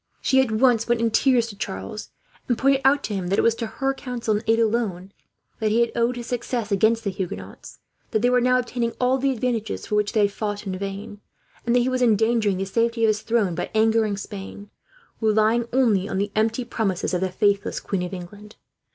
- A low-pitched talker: No, high, 220 Hz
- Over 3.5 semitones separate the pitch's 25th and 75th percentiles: No, average, 2.9 semitones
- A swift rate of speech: Yes, fast, 225 wpm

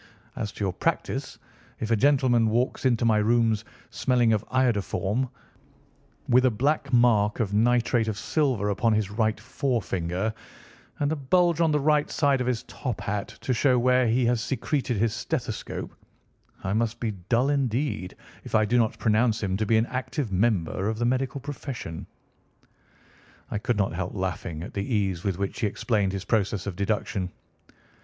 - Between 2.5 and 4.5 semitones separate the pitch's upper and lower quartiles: Yes, average, 3.7 semitones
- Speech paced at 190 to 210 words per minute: No, average, 175 wpm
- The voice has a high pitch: No, low, 115 Hz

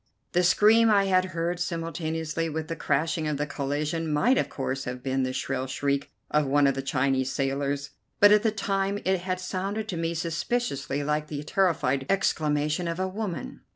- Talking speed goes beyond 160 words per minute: Yes, average, 190 wpm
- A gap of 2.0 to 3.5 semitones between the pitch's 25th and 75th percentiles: No, average, 4.7 semitones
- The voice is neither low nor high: Yes, medium, 160 Hz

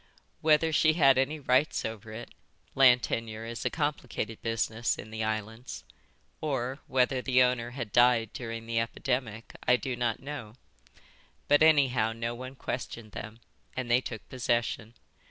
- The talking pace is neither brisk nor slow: Yes, average, 155 wpm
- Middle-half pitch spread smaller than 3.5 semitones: Yes, narrow, 2.5 semitones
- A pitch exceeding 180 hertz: No, low, 120 Hz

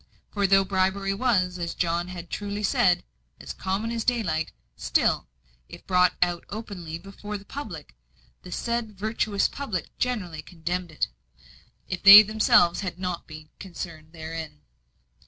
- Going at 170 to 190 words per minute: No, average, 140 wpm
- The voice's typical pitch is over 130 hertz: Yes, medium, 185 Hz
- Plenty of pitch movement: No, average, 3.3 semitones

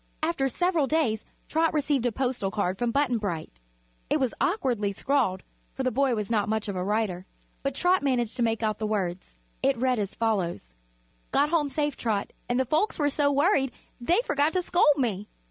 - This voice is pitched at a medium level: No, very high, 250 Hz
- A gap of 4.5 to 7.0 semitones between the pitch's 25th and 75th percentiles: Yes, wide, 5.4 semitones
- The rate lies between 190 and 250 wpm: Yes, average, 195 wpm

